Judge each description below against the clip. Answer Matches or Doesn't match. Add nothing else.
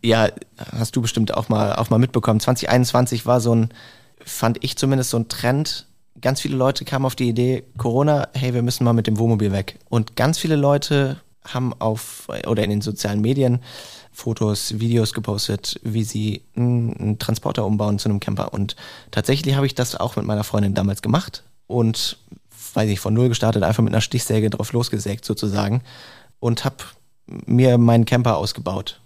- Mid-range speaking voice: Doesn't match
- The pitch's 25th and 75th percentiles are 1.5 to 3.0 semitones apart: Matches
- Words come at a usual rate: Matches